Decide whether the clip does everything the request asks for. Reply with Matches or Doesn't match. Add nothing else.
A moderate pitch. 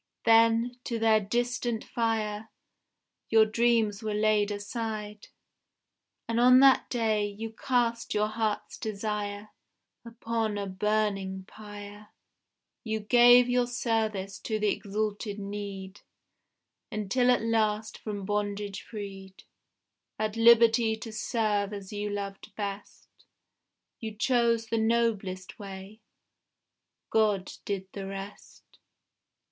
Doesn't match